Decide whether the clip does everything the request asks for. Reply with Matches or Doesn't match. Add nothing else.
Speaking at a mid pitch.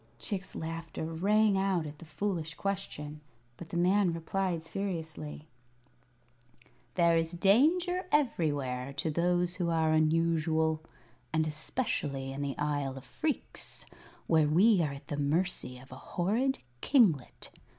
Matches